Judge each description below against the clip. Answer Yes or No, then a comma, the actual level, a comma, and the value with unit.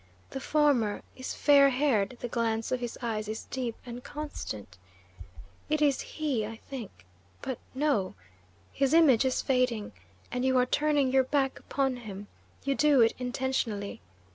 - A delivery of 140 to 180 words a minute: Yes, average, 155 wpm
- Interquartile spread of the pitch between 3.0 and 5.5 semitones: Yes, average, 3.6 semitones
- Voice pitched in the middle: No, very high, 255 Hz